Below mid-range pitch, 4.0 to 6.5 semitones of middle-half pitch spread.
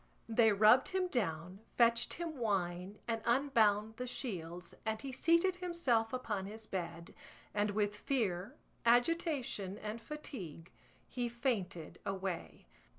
No: high, 220 Hz; average, 4.9 semitones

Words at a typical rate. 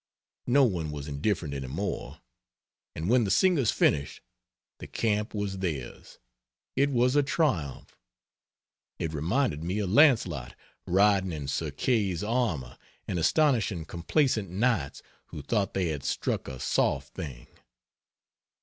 No: slow, 130 wpm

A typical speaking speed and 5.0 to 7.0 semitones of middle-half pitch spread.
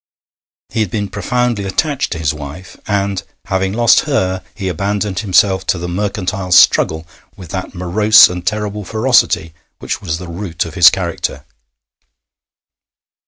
No: average, 145 wpm; average, 2.7 semitones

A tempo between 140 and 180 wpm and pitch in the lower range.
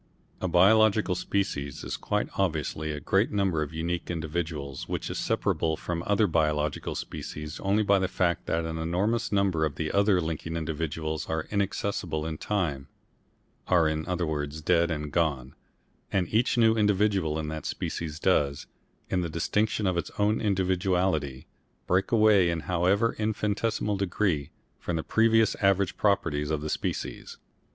Yes: average, 155 wpm; very low, 85 Hz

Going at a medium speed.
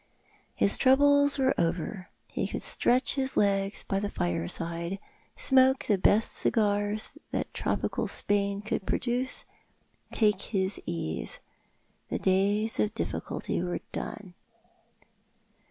No: slow, 115 wpm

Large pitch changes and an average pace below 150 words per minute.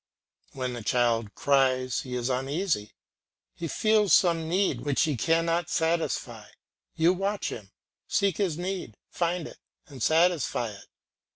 Yes: wide, 5.7 semitones; slow, 135 wpm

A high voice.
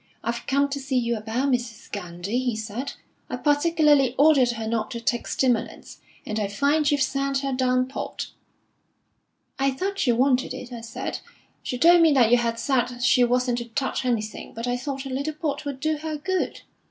Yes: very high, 255 Hz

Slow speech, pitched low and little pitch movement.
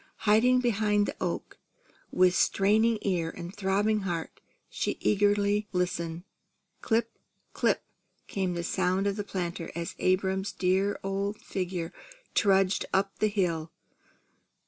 No: slow, 125 wpm; high, 195 Hz; narrow, 2.3 semitones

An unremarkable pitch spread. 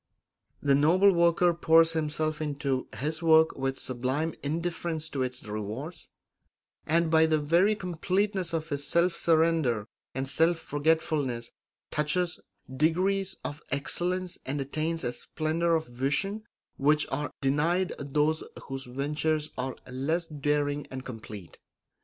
Yes: average, 3.4 semitones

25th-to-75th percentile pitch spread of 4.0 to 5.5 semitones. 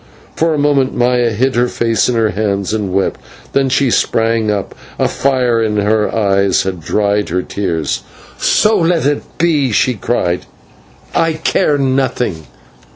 Yes: average, 4.9 semitones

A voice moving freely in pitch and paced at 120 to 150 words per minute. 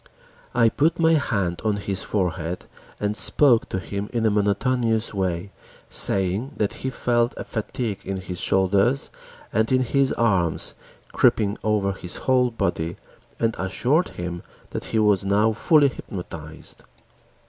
No: average, 4.1 semitones; average, 145 wpm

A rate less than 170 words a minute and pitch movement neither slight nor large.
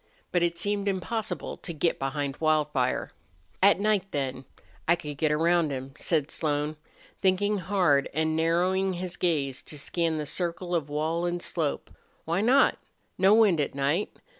Yes: average, 160 wpm; average, 3.8 semitones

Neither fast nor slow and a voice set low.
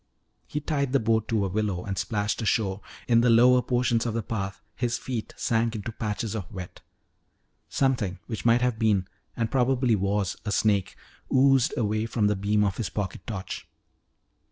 Yes: average, 180 wpm; low, 110 Hz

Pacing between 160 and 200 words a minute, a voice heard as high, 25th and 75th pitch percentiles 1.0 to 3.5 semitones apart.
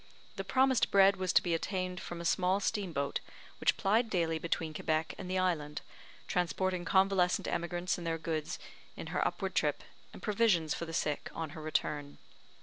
No: average, 180 wpm; medium, 175 Hz; average, 2.8 semitones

